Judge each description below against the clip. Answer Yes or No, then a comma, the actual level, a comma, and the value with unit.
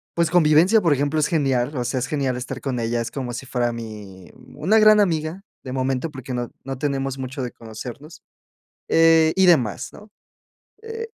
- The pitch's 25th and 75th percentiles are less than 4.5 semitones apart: No, average, 4.8 semitones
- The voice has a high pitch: No, low, 135 Hz